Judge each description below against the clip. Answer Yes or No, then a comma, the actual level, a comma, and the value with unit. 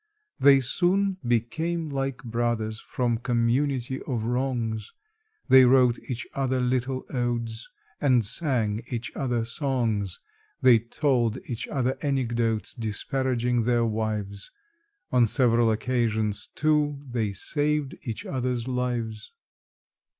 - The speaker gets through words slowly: Yes, slow, 110 wpm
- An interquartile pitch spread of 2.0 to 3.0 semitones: Yes, narrow, 2.6 semitones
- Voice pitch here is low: Yes, low, 120 Hz